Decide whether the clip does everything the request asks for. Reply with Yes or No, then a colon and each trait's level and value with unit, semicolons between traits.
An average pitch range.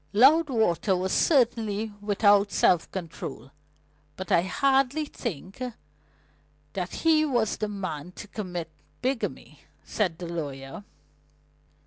No: wide, 5.8 semitones